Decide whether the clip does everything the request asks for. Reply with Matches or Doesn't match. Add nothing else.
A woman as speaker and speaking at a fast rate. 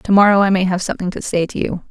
Matches